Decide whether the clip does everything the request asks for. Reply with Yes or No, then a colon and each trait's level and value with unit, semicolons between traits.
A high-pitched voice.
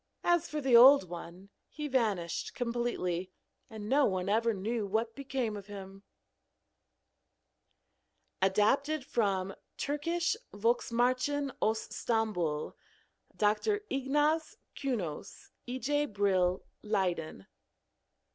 Yes: high, 225 Hz